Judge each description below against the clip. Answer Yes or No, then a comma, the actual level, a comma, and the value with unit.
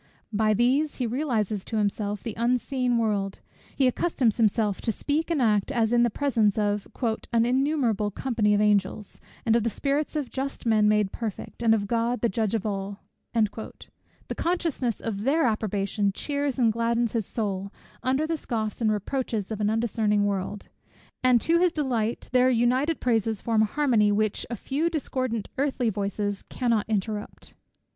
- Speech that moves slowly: No, average, 170 wpm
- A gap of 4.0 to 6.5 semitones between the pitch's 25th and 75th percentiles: No, average, 3.5 semitones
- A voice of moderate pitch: No, high, 225 Hz